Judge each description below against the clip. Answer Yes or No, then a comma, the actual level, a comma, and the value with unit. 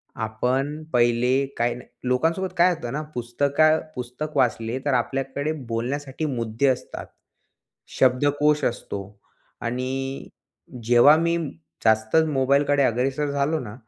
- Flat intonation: No, average, 3.3 semitones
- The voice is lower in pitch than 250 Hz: Yes, low, 135 Hz